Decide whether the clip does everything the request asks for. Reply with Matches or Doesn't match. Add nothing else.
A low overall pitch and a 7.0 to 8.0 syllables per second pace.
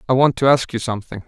Matches